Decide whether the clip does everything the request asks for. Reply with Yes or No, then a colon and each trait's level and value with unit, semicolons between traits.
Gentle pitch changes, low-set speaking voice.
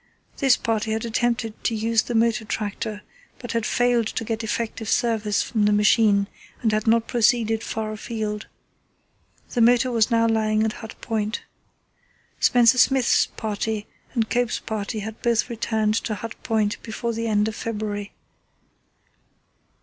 No: narrow, 1.5 semitones; high, 225 Hz